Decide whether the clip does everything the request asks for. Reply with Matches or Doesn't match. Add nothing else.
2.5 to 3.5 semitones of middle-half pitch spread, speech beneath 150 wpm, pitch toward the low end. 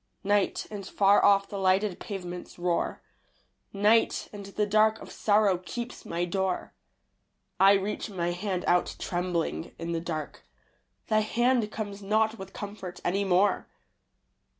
Doesn't match